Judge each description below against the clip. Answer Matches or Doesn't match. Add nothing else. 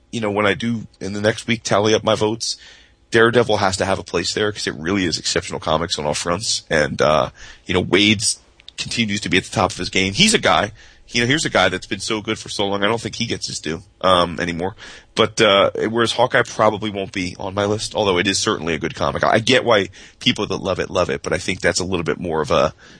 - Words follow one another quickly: Matches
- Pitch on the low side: Matches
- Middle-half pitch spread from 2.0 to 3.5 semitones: Matches